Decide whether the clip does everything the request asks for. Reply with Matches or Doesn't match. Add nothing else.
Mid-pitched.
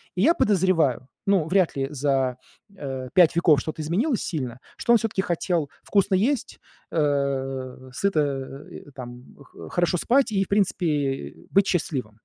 Matches